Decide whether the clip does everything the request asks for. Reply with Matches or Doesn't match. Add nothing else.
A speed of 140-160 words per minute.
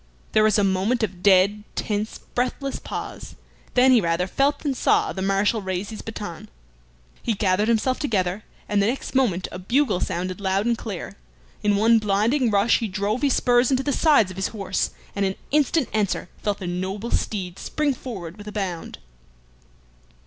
Doesn't match